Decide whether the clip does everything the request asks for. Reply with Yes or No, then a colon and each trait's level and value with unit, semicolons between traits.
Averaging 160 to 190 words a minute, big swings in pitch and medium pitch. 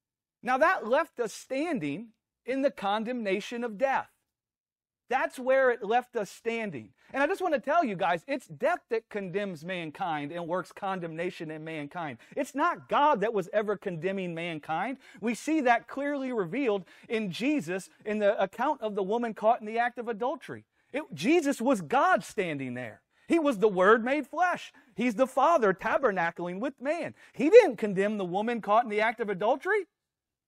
No: average, 175 wpm; wide, 6.2 semitones; high, 225 Hz